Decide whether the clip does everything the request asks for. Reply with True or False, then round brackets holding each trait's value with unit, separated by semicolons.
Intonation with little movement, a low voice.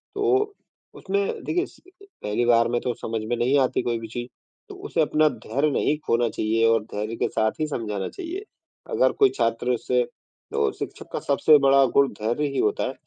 False (5.4 semitones; 125 Hz)